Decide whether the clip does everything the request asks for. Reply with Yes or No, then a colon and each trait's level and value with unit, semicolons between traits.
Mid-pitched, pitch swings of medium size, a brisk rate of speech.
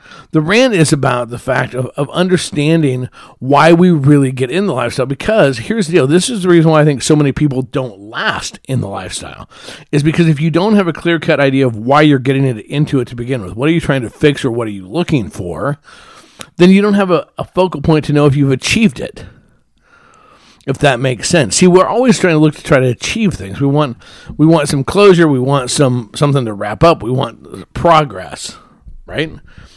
Yes: medium, 145 Hz; average, 4.8 semitones; fast, 225 wpm